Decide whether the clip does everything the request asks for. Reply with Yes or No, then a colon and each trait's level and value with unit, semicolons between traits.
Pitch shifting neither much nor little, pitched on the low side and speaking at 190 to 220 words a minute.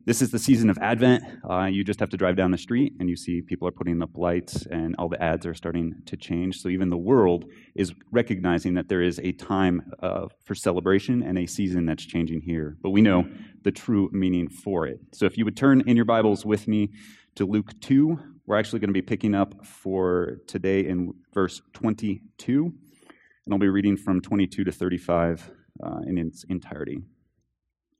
Yes: average, 3.4 semitones; very low, 95 Hz; fast, 205 wpm